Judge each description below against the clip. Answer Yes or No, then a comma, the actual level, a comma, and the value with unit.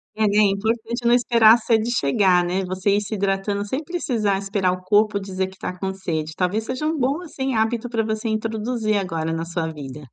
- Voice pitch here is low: No, high, 205 Hz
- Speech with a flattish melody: No, average, 3.5 semitones